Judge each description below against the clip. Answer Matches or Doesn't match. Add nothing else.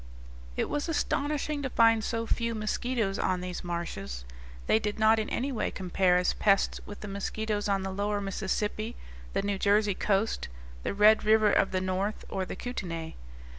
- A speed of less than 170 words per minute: Doesn't match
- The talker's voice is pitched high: Matches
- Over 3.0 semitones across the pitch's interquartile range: Doesn't match